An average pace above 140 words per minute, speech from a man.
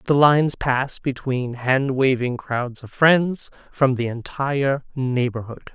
No: slow, 135 wpm; male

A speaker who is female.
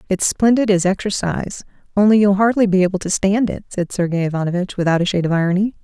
Yes: female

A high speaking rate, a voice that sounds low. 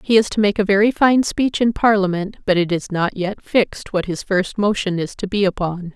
No: fast, 240 wpm; high, 200 Hz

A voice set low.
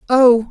No: high, 245 Hz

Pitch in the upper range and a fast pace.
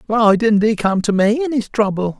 Yes: high, 215 Hz; fast, 245 wpm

